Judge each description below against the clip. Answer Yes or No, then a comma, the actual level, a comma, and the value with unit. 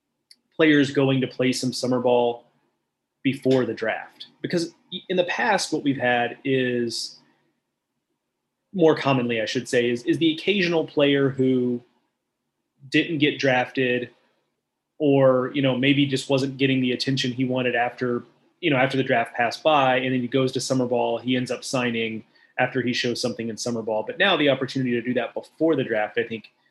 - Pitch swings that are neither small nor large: No, narrow, 2.1 semitones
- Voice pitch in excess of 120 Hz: Yes, low, 130 Hz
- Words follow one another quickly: No, average, 180 wpm